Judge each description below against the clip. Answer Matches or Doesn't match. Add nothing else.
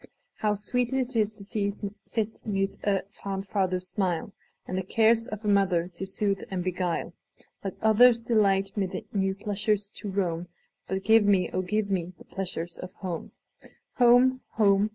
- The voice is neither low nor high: Doesn't match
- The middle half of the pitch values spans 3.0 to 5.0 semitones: Doesn't match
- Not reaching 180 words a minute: Matches